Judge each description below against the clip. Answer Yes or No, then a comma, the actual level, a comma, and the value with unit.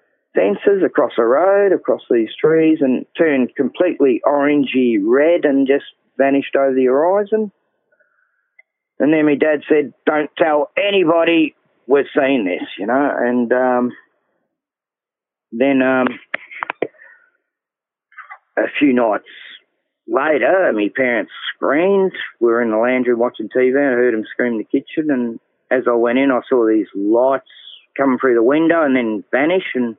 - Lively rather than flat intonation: Yes, wide, 7.8 semitones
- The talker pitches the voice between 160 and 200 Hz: No, medium, 140 Hz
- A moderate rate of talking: Yes, average, 150 wpm